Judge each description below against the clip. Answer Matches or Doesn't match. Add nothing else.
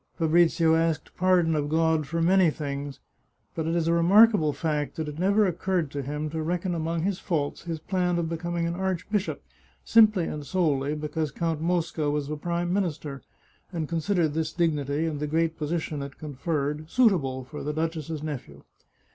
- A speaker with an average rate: Matches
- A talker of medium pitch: Matches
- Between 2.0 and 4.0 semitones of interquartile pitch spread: Matches